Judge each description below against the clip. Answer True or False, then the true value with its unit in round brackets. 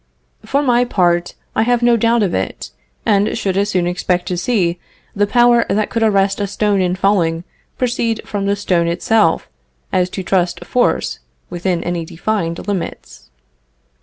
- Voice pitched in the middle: False (195 Hz)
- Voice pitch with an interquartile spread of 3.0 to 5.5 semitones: True (4.0 semitones)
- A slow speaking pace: False (165 wpm)